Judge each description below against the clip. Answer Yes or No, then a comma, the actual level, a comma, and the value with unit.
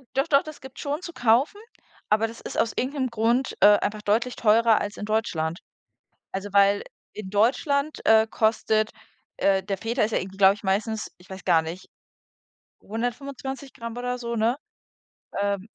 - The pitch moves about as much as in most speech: Yes, average, 3.5 semitones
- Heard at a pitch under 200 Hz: No, high, 220 Hz